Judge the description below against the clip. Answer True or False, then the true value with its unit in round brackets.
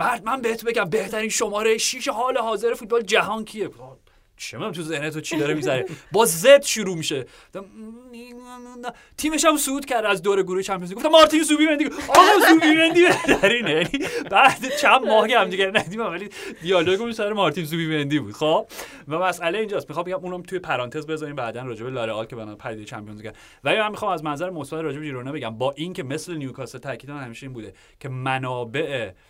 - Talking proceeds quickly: True (195 wpm)